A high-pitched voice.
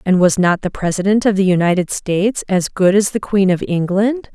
Yes: high, 195 Hz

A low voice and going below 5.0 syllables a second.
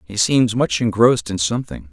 No: low, 110 Hz; 5.5 syllables/s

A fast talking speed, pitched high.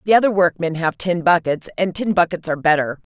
No: fast, 210 wpm; medium, 170 Hz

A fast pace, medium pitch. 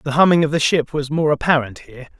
Yes: fast, 245 wpm; medium, 145 Hz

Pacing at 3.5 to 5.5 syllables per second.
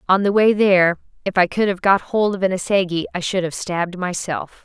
No: 5.7 syllables/s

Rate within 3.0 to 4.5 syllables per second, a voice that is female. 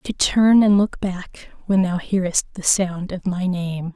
Yes: 4.0 syllables/s; female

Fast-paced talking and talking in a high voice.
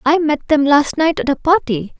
Yes: fast, 240 wpm; very high, 295 Hz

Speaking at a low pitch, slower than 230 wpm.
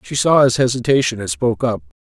Yes: low, 125 Hz; fast, 205 wpm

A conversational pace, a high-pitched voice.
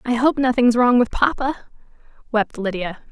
Yes: average, 175 wpm; high, 240 Hz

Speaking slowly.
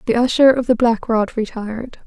No: fast, 205 wpm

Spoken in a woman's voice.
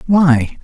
No: male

